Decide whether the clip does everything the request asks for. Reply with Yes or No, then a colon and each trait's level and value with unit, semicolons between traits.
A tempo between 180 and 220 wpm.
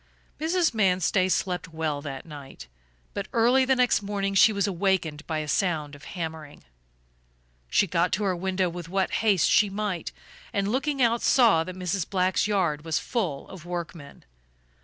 No: average, 165 wpm